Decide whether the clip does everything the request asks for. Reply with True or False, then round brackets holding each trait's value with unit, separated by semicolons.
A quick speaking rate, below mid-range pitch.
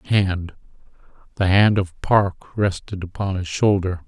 False (145 wpm; 95 Hz)